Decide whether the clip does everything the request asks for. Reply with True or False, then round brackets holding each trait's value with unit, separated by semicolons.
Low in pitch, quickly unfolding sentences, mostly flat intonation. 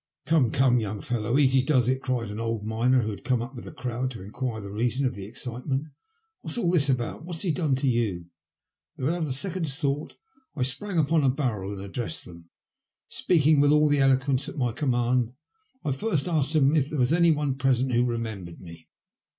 False (130 Hz; 220 wpm; 4.1 semitones)